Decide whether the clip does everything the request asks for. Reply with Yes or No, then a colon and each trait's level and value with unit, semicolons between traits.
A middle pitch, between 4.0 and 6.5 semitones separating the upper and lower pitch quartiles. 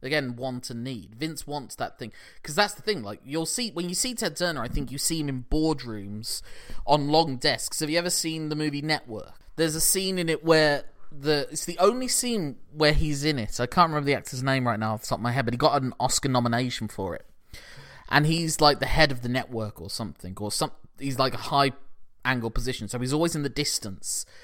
Yes: medium, 145 Hz; average, 4.3 semitones